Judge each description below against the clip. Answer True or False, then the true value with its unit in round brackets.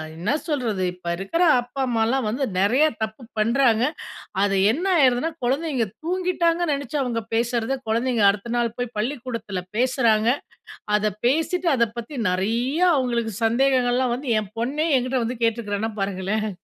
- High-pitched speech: True (240 Hz)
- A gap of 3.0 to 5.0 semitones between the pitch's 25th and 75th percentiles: True (3.6 semitones)